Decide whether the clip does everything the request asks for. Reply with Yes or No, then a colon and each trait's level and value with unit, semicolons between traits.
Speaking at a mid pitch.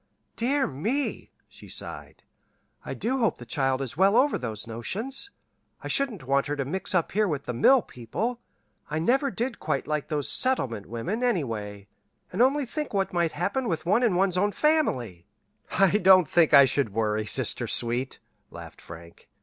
Yes: medium, 175 Hz